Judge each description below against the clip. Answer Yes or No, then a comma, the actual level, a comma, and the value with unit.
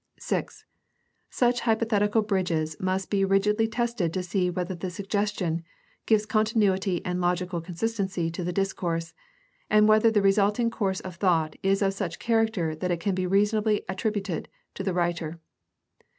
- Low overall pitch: No, high, 195 Hz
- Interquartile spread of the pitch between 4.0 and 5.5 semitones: No, average, 3.0 semitones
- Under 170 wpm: Yes, average, 150 wpm